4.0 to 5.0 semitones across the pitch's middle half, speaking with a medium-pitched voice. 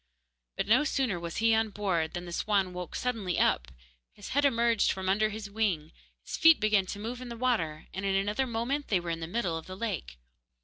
No: average, 4.5 semitones; high, 205 Hz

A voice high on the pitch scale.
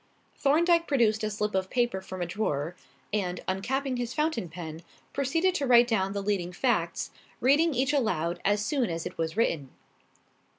Yes: high, 215 Hz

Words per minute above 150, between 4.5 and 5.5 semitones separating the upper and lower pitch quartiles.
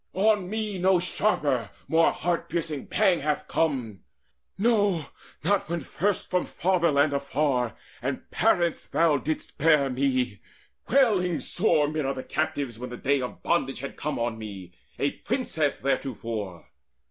No: average, 140 wpm; average, 5.2 semitones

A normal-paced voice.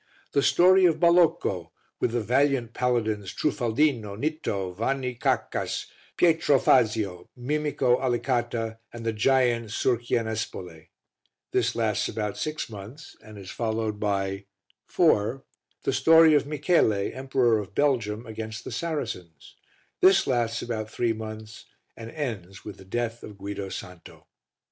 No: slow, 130 wpm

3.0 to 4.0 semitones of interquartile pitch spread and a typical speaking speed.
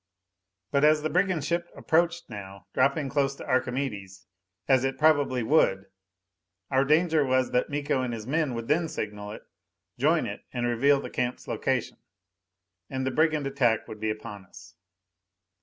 No: average, 4.6 semitones; average, 160 wpm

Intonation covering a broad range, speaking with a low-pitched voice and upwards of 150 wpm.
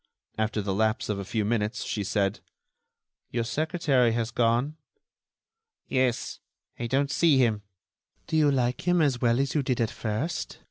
No: average, 4.1 semitones; low, 120 Hz; average, 165 wpm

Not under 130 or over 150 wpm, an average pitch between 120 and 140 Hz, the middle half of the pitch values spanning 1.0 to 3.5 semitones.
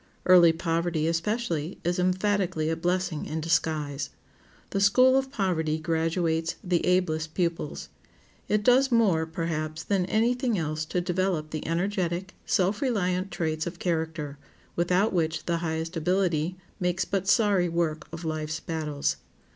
No: average, 140 wpm; medium, 170 Hz; average, 2.9 semitones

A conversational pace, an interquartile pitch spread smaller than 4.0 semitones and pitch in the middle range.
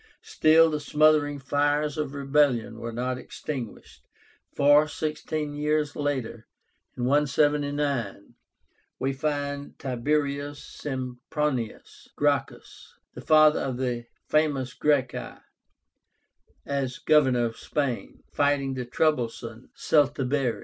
No: slow, 95 wpm; average, 2.7 semitones; medium, 145 Hz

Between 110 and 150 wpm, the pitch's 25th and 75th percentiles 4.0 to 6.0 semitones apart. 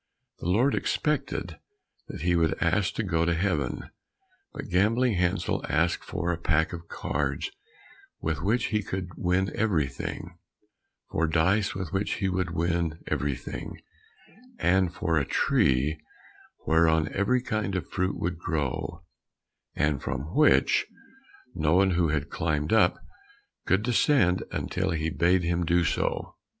No: average, 140 wpm; average, 3.2 semitones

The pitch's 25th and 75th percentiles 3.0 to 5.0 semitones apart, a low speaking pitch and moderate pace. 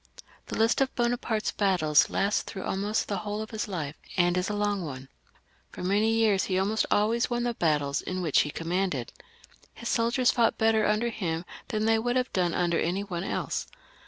No: average, 4.1 semitones; high, 205 Hz; average, 195 wpm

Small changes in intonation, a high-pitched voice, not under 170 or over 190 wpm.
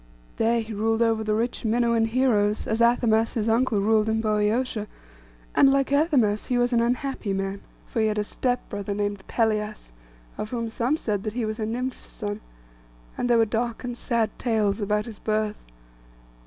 Yes: narrow, 2.2 semitones; high, 225 Hz; average, 185 wpm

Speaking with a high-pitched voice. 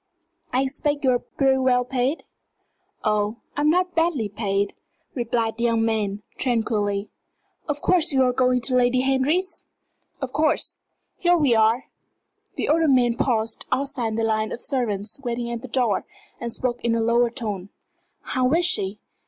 Yes: high, 245 Hz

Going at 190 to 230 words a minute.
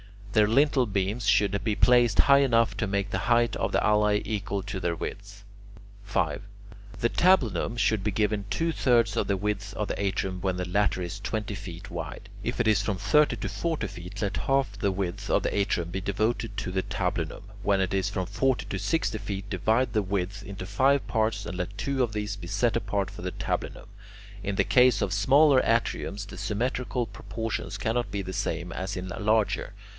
Yes: average, 200 wpm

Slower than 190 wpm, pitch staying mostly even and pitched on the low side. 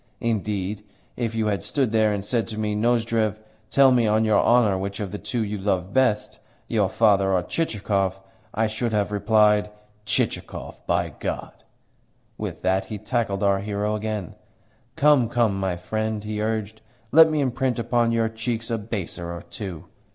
Yes: average, 170 wpm; narrow, 2.3 semitones; low, 105 Hz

